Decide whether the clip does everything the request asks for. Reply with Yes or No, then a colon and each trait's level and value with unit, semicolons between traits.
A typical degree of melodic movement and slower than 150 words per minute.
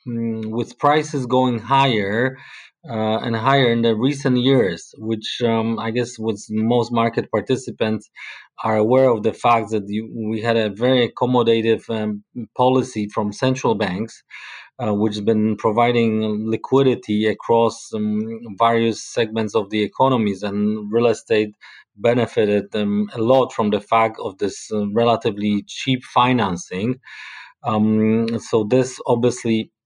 No: narrow, 2.1 semitones; average, 140 wpm